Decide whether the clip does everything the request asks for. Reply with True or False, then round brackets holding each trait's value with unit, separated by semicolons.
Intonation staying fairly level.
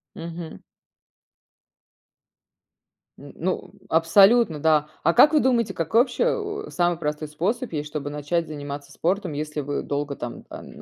False (4.0 semitones)